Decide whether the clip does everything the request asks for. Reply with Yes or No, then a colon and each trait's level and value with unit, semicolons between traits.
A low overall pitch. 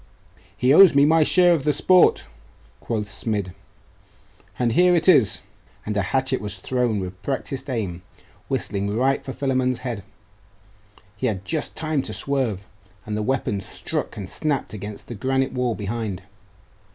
Yes: low, 125 Hz